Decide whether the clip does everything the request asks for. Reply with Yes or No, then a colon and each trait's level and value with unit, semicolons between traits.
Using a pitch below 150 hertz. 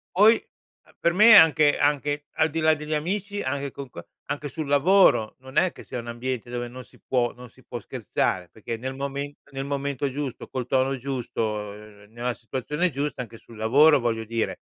Yes: low, 135 Hz